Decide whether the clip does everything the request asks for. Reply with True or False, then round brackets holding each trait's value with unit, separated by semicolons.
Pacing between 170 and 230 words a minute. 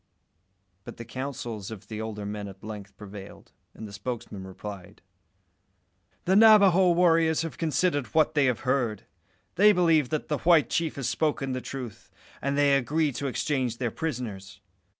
False (160 wpm)